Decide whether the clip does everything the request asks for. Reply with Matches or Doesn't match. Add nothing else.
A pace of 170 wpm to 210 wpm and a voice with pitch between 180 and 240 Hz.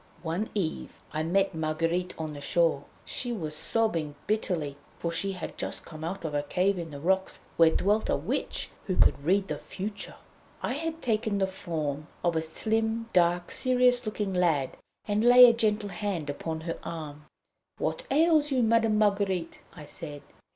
Matches